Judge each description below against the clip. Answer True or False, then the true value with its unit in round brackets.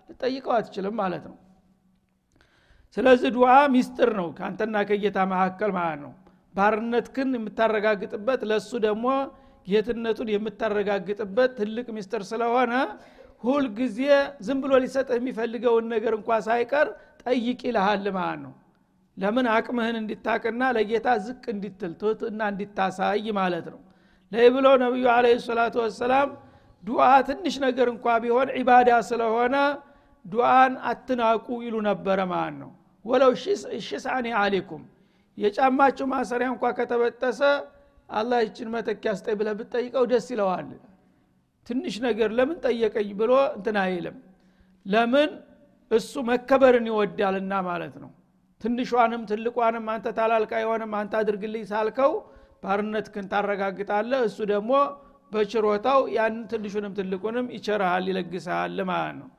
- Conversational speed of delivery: False (115 wpm)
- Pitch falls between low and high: False (225 Hz)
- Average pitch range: True (3.4 semitones)